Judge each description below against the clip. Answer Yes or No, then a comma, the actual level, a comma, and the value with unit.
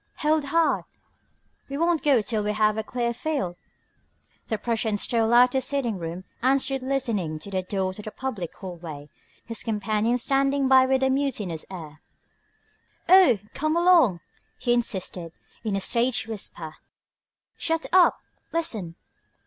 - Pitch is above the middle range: Yes, high, 235 Hz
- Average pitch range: No, wide, 5.9 semitones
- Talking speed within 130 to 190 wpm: Yes, average, 150 wpm